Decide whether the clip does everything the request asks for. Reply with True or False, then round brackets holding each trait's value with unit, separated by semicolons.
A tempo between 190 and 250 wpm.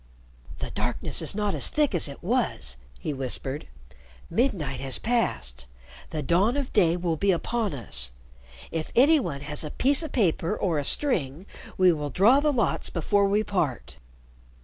False (170 wpm)